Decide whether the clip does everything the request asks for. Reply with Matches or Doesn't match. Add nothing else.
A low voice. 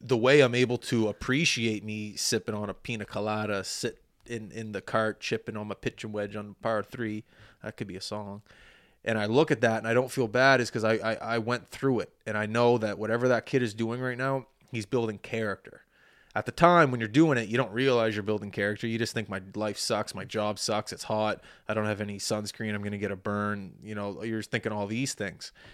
Matches